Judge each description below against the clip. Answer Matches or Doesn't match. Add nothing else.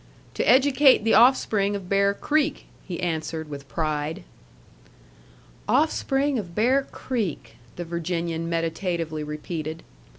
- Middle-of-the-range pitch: Matches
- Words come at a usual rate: Doesn't match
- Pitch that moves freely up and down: Matches